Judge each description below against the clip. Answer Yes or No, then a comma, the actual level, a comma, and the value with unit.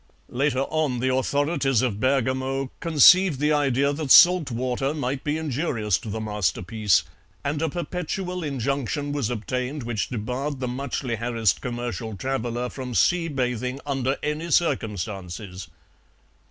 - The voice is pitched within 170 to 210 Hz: No, low, 130 Hz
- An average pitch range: Yes, average, 3.6 semitones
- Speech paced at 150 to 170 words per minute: No, slow, 135 wpm